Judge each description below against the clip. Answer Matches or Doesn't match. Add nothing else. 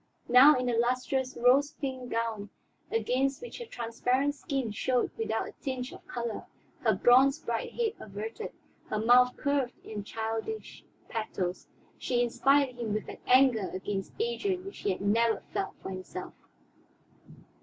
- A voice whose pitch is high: Matches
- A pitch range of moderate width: Matches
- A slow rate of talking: Doesn't match